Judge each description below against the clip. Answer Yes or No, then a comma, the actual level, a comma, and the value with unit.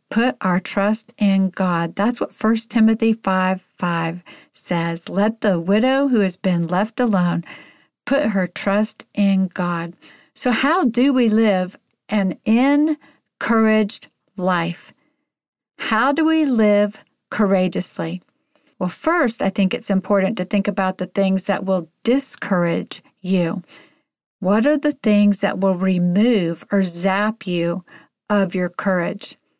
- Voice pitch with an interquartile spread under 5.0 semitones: Yes, average, 3.5 semitones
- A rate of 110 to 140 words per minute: Yes, slow, 135 wpm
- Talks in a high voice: Yes, high, 200 Hz